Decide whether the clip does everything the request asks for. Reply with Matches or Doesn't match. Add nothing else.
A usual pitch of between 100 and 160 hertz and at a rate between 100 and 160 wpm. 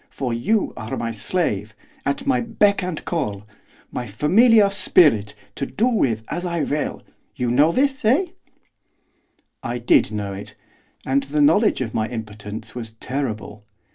Matches